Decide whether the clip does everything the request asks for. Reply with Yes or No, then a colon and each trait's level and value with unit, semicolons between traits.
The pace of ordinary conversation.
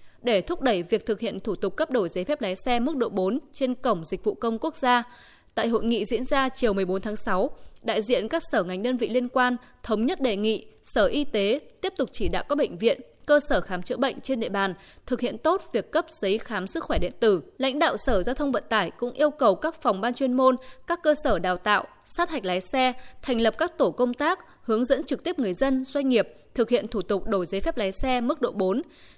No: fast, 255 wpm